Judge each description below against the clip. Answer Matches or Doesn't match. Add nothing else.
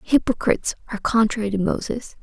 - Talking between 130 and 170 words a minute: Matches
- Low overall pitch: Doesn't match